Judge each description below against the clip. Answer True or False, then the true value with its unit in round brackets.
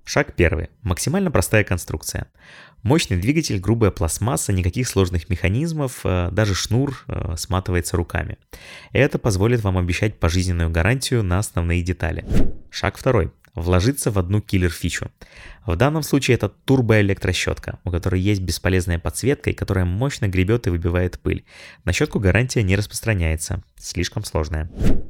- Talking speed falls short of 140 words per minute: True (130 wpm)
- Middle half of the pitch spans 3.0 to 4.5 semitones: True (4.2 semitones)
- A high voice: False (95 Hz)